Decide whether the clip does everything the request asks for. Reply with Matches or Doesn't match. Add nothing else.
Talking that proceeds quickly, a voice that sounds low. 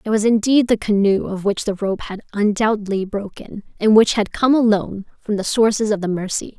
Doesn't match